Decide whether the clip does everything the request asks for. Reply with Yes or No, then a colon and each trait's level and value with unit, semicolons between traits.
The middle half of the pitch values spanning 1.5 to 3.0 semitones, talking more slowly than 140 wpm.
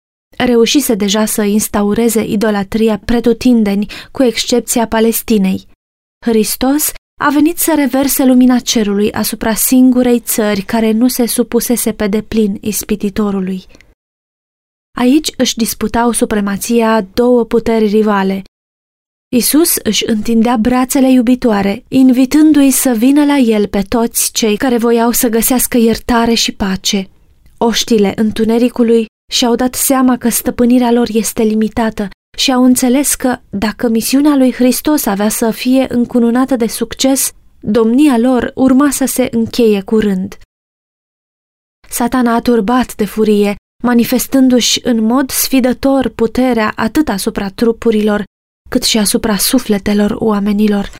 Yes: average, 2.7 semitones; average, 120 wpm